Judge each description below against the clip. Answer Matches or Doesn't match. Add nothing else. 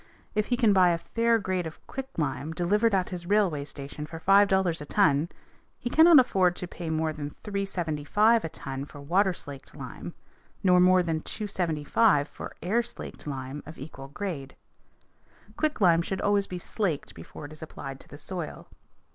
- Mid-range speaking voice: Matches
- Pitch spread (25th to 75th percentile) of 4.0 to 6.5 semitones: Matches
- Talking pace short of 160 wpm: Doesn't match